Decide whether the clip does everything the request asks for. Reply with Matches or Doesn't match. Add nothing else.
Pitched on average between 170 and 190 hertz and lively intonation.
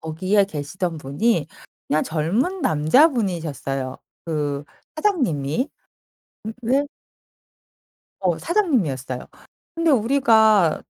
Matches